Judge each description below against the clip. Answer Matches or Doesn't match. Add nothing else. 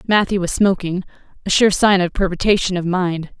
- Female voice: Matches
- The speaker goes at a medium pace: Matches